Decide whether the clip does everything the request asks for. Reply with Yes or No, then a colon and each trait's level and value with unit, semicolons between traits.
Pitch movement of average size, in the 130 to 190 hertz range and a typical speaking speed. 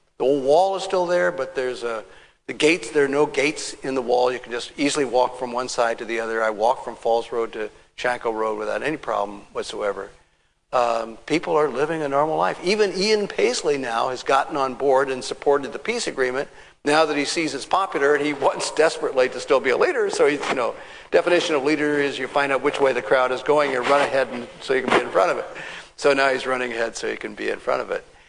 No: average, 4.2 semitones; medium, 140 Hz; fast, 250 wpm